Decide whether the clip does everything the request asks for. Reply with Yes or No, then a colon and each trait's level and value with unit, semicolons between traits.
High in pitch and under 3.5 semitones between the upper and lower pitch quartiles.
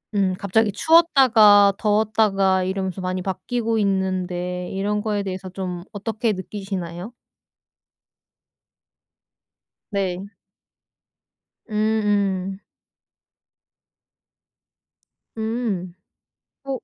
Yes: high, 195 Hz; narrow, 2.5 semitones